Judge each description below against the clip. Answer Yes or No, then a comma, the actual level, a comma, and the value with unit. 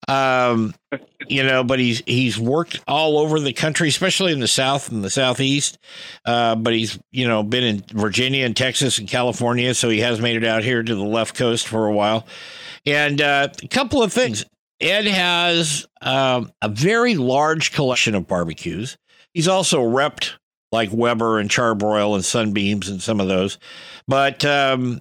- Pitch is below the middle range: Yes, low, 125 Hz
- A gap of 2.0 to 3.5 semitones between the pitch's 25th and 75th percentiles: No, average, 4.4 semitones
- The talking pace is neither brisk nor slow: Yes, average, 180 wpm